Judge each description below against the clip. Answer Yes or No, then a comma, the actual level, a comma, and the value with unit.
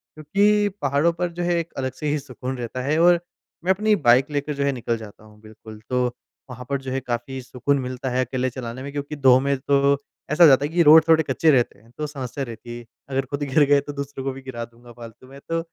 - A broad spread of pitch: No, average, 3.0 semitones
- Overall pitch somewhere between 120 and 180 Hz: Yes, low, 135 Hz